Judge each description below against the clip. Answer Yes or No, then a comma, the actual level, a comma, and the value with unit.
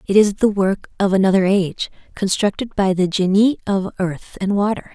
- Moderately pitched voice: No, high, 195 Hz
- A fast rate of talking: No, average, 180 wpm